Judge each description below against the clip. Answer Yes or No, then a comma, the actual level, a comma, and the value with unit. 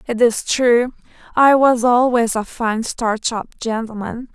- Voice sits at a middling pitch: No, high, 235 Hz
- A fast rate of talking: No, average, 150 wpm